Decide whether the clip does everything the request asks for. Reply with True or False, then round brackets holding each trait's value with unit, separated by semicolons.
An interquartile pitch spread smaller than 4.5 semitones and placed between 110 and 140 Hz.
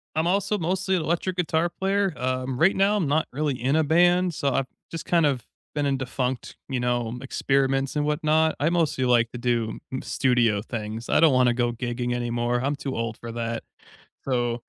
False (4.8 semitones; 135 Hz)